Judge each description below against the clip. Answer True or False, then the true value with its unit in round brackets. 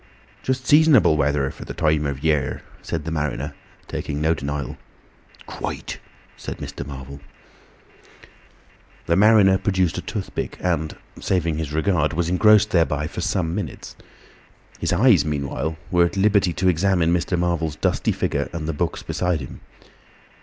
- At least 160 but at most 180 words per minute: False (145 wpm)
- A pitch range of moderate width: True (3.7 semitones)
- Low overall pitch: True (85 Hz)